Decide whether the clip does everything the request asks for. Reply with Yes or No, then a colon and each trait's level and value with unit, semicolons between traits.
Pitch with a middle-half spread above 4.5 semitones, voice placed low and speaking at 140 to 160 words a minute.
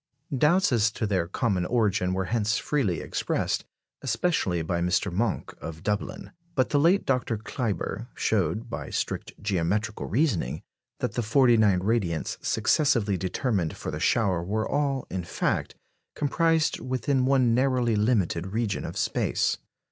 Yes: wide, 5.4 semitones; low, 110 Hz; average, 145 wpm